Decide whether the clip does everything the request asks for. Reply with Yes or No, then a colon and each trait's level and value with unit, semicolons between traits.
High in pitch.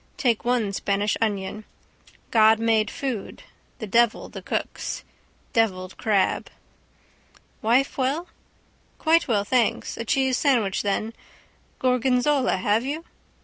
Yes: high, 225 Hz